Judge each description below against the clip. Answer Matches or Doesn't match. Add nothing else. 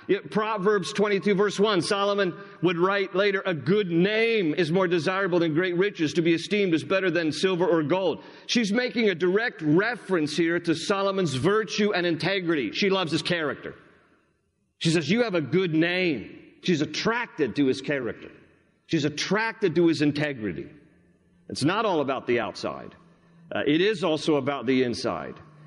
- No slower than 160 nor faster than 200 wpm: Matches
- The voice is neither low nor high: Matches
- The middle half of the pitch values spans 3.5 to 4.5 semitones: Matches